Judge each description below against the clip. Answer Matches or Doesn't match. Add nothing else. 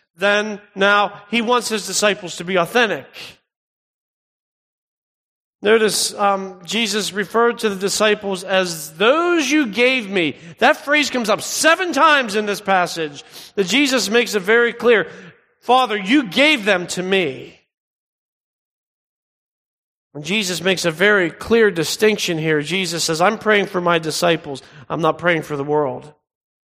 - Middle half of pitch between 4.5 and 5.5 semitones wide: Matches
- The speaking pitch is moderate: Doesn't match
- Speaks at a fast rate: Doesn't match